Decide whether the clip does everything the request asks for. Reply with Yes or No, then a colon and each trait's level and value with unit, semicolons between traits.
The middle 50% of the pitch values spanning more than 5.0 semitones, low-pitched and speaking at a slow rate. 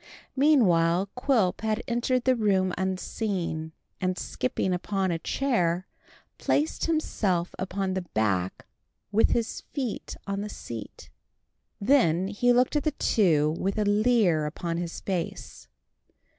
No: wide, 5.4 semitones; high, 195 Hz; slow, 130 wpm